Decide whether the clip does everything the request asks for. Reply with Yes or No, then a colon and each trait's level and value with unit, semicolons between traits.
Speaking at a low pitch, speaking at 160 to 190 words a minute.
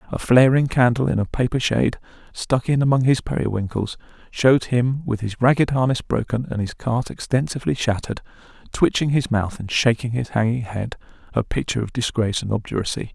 Yes: low, 120 Hz; average, 175 wpm